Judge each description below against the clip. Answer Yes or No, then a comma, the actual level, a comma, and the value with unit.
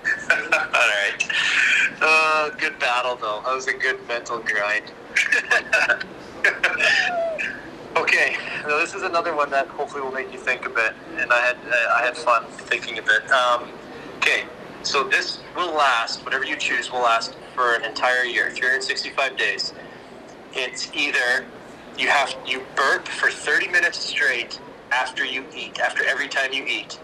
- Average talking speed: Yes, average, 160 wpm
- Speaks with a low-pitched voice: No, medium, 145 Hz